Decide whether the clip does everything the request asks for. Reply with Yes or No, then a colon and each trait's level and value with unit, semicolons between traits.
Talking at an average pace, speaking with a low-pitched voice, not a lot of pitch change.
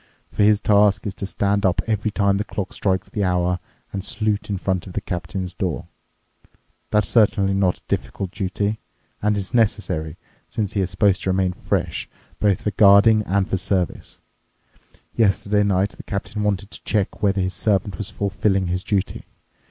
Yes: average, 175 wpm; low, 100 Hz; narrow, 1.9 semitones